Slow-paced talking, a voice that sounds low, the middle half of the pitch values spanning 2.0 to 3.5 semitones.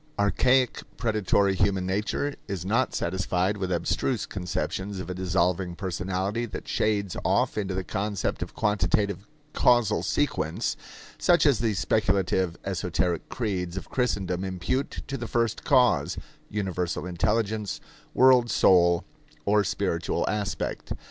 Yes: slow, 125 wpm; low, 100 Hz; average, 3.1 semitones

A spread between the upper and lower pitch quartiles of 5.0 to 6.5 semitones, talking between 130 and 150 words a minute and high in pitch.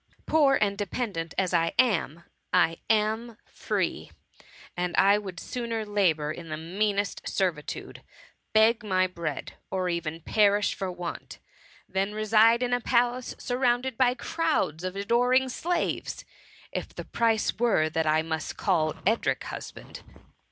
Yes: average, 5.3 semitones; average, 140 wpm; high, 205 Hz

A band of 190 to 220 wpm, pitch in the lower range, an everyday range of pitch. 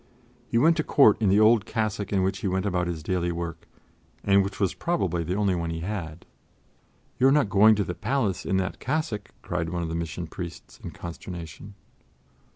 Yes: fast, 205 wpm; very low, 95 Hz; average, 3.7 semitones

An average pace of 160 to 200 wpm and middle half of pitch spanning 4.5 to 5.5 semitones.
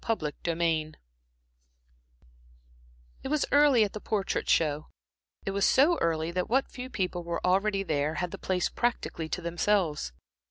No: average, 150 wpm; average, 4.9 semitones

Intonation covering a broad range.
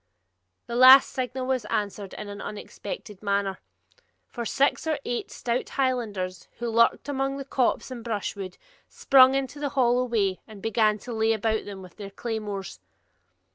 No: average, 4.1 semitones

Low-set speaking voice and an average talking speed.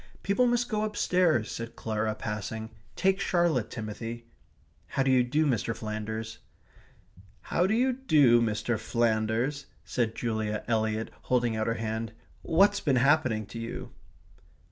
No: low, 115 Hz; slow, 130 wpm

